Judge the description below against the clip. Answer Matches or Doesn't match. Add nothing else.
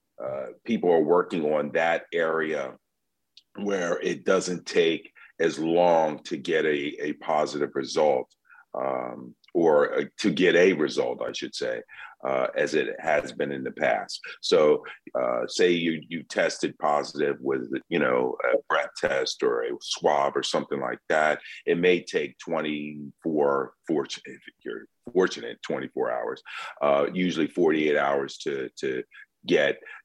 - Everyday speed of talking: Matches